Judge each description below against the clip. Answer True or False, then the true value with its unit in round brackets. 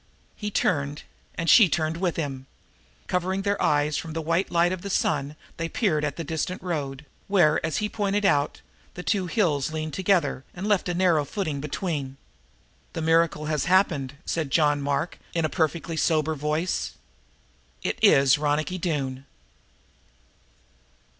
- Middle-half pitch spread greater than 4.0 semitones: False (3.6 semitones)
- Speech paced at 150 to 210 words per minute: True (160 wpm)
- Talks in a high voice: False (160 Hz)